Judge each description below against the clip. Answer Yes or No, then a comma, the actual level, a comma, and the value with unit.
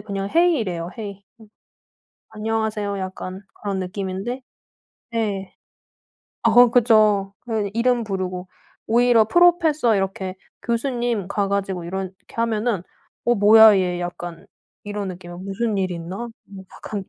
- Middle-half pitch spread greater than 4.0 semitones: No, average, 3.4 semitones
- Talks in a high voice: Yes, high, 205 Hz